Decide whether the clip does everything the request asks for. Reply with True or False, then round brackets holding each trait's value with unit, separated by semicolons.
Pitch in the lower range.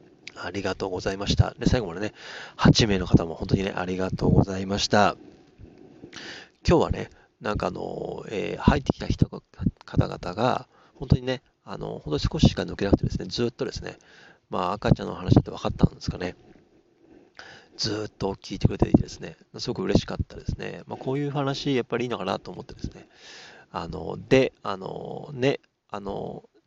True (115 Hz)